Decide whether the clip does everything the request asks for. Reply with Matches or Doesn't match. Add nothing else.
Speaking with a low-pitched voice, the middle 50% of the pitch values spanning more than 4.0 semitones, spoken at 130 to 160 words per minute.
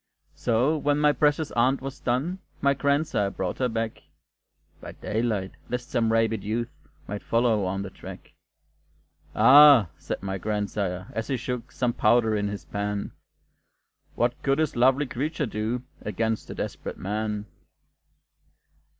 Matches